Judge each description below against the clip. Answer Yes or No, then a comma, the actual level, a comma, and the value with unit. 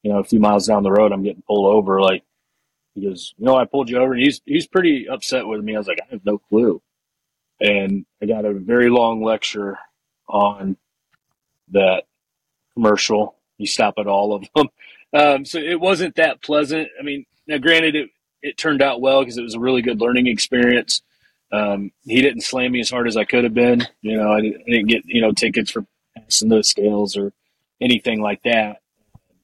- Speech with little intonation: No, average, 3.8 semitones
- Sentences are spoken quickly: Yes, fast, 210 wpm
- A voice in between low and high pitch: No, low, 115 Hz